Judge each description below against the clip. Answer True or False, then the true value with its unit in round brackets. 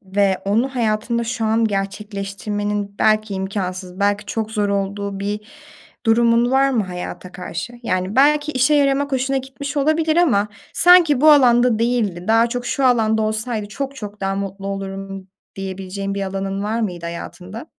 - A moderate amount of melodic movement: True (4.0 semitones)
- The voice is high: True (215 Hz)